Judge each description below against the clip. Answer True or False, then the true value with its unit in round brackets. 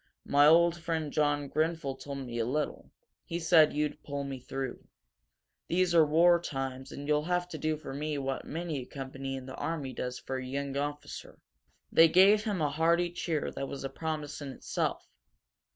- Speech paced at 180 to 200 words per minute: True (190 wpm)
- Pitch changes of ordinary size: True (3.4 semitones)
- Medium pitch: True (150 Hz)